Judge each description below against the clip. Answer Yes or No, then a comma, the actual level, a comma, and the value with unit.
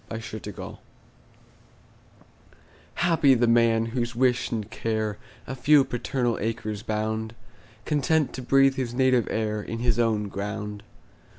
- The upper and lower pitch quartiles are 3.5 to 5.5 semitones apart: No, average, 2.9 semitones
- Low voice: Yes, low, 115 Hz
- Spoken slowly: Yes, slow, 130 wpm